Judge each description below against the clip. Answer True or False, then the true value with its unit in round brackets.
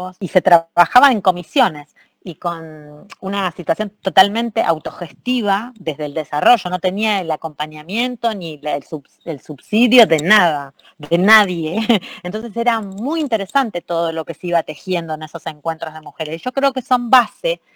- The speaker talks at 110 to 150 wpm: False (160 wpm)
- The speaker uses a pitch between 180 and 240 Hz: True (185 Hz)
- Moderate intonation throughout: False (6.0 semitones)